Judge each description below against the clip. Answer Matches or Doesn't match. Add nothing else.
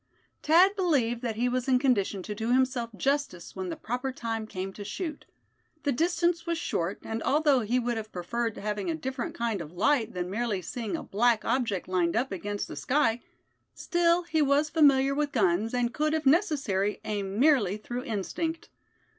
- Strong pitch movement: Matches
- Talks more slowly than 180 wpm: Doesn't match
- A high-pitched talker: Matches